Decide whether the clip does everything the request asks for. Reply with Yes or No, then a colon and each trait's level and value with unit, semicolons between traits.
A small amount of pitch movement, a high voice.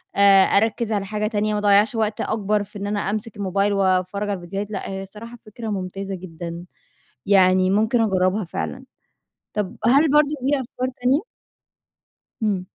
Yes: narrow, 2.2 semitones; high, 205 Hz